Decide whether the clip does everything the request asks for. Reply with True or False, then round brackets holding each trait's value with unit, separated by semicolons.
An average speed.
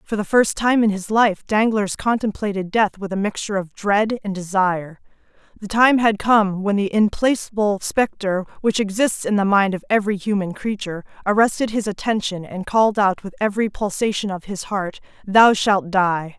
True (180 wpm)